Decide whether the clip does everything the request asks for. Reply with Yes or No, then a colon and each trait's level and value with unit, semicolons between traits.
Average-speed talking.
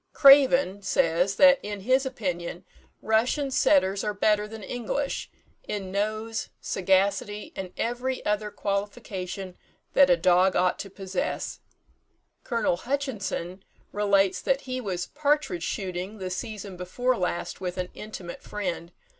No: slow, 130 wpm